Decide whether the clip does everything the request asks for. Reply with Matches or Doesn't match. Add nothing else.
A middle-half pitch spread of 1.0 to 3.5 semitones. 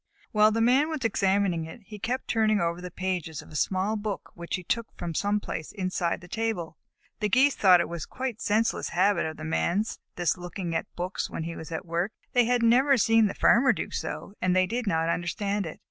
Doesn't match